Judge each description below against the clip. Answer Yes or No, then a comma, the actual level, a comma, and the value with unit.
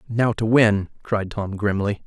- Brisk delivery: No, average, 175 wpm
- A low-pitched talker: Yes, low, 105 Hz